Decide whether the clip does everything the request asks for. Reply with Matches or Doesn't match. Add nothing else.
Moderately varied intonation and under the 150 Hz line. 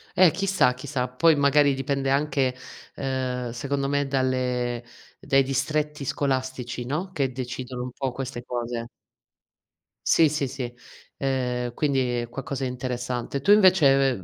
Doesn't match